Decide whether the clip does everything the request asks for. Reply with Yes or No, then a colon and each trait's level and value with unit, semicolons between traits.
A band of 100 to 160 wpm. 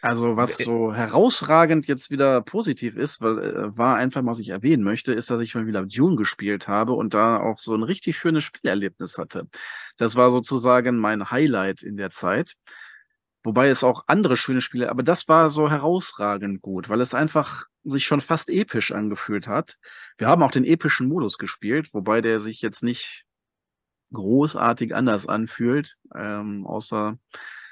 No: average, 170 wpm